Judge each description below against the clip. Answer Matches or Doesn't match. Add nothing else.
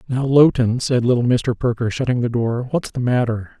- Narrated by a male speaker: Matches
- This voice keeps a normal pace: Matches